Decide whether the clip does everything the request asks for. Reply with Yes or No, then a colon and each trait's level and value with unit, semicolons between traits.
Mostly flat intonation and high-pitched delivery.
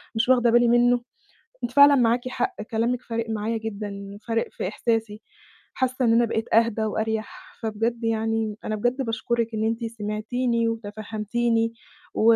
Yes: narrow, 1.6 semitones; high, 230 Hz